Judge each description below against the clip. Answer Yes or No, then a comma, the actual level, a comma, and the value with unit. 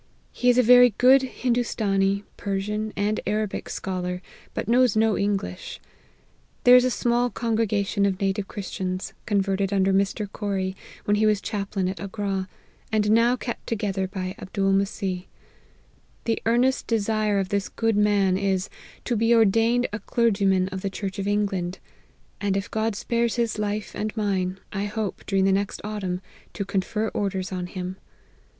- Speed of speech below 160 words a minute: No, average, 165 wpm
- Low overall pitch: No, high, 205 Hz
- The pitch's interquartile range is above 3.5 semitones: No, narrow, 2.5 semitones